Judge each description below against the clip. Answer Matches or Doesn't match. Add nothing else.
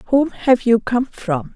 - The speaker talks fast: Doesn't match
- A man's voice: Doesn't match